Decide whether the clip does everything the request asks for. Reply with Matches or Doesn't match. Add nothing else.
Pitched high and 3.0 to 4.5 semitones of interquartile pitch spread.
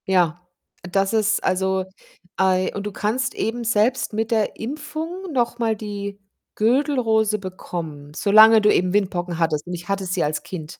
Matches